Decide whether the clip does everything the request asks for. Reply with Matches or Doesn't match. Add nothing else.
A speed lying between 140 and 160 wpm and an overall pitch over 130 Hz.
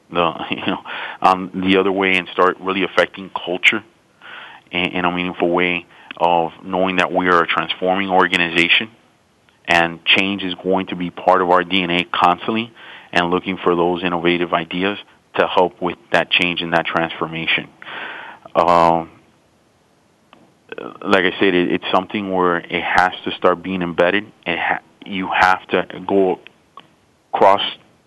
Doesn't match